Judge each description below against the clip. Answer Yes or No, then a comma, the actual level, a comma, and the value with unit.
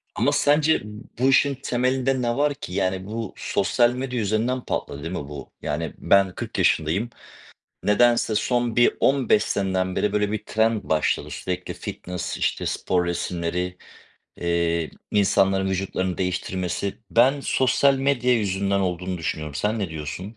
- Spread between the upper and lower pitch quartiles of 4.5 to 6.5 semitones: Yes, average, 5.1 semitones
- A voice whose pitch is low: Yes, low, 100 Hz